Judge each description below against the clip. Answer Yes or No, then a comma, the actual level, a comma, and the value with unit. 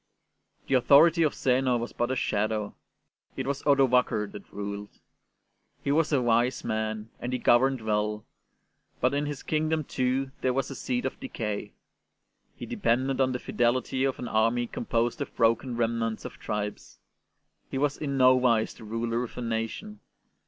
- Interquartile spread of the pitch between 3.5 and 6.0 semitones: No, average, 3.1 semitones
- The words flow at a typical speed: Yes, average, 165 wpm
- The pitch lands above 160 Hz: No, low, 125 Hz